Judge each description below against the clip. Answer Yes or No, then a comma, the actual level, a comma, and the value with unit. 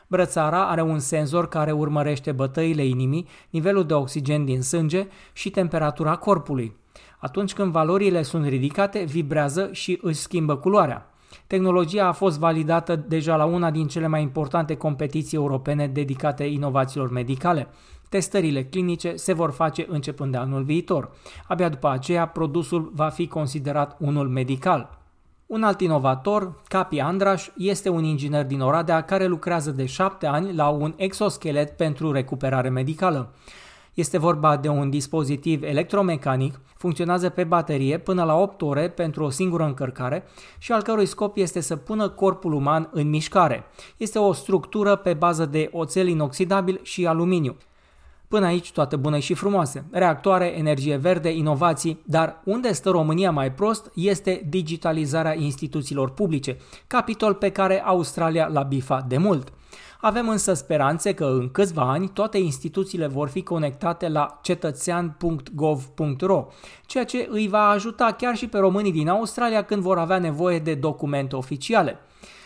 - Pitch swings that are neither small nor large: Yes, average, 4.1 semitones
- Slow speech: No, average, 150 wpm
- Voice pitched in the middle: Yes, medium, 165 Hz